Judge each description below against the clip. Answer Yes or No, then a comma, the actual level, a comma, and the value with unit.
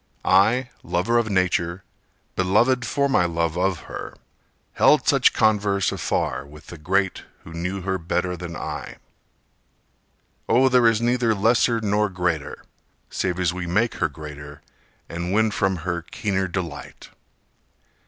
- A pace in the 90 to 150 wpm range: Yes, average, 140 wpm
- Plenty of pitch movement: No, average, 4.1 semitones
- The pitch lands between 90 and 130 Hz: Yes, very low, 95 Hz